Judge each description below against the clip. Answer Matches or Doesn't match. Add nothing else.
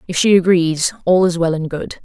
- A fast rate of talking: Matches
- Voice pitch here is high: Doesn't match